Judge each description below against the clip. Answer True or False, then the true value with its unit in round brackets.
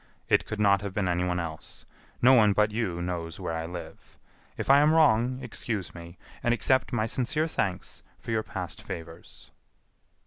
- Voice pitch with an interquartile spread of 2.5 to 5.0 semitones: False (5.5 semitones)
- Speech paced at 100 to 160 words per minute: False (175 wpm)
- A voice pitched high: False (100 Hz)